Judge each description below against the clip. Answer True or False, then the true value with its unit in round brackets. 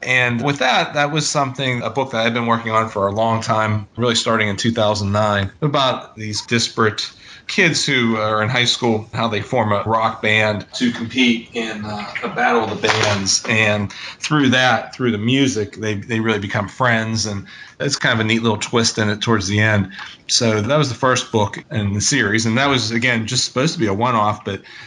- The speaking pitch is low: True (115 Hz)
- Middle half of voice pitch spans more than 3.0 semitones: False (2.7 semitones)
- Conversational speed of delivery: False (215 wpm)